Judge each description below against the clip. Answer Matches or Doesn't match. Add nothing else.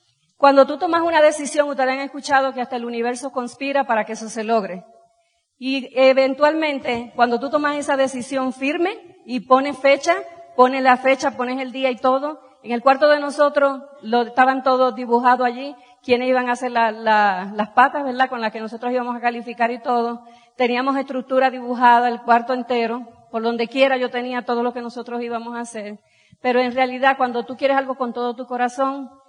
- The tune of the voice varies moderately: Doesn't match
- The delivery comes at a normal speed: Doesn't match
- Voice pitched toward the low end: Doesn't match